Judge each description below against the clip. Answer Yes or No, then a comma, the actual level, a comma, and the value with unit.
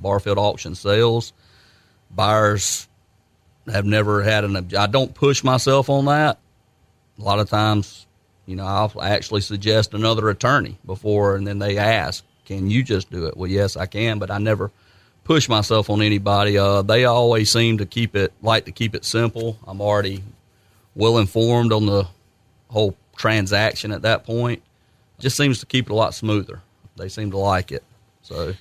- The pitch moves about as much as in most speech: No, narrow, 2.3 semitones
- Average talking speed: Yes, average, 175 wpm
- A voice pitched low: Yes, low, 105 Hz